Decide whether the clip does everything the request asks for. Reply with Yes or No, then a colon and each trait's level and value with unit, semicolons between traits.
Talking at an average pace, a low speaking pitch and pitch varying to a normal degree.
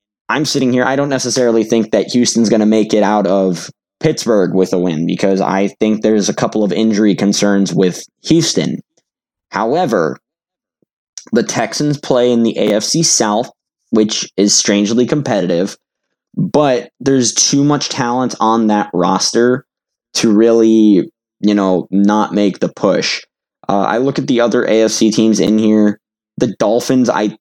Yes: average, 155 wpm; low, 110 Hz; average, 3.1 semitones